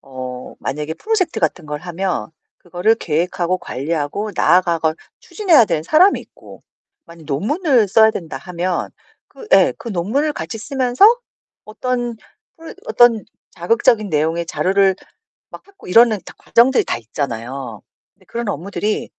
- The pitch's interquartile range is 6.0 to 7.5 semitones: Yes, wide, 7.0 semitones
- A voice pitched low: No, high, 190 Hz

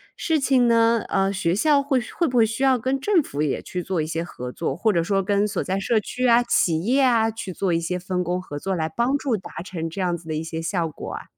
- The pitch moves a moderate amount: No, wide, 6.0 semitones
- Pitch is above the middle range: Yes, high, 195 Hz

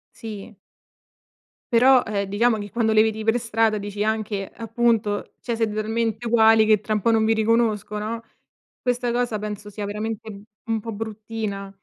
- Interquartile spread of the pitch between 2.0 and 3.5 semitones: No, narrow, 1.5 semitones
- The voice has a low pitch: No, high, 220 Hz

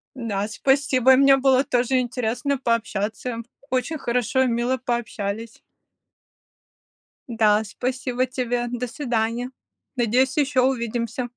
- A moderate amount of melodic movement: No, narrow, 2.1 semitones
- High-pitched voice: Yes, high, 245 Hz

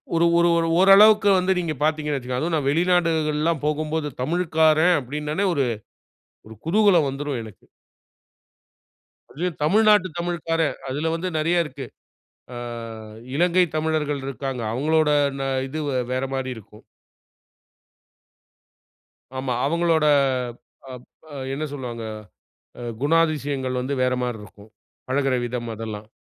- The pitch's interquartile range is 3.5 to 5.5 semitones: Yes, average, 4.1 semitones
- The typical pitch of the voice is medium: Yes, medium, 155 Hz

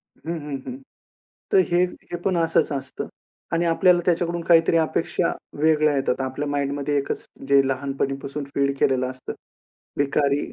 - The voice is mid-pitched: Yes, medium, 145 Hz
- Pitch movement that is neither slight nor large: Yes, average, 3.2 semitones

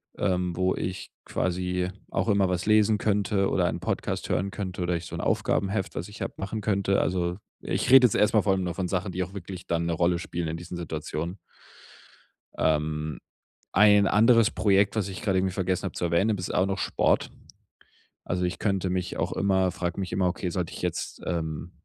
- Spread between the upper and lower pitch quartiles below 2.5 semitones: Yes, narrow, 2.1 semitones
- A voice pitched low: Yes, very low, 95 Hz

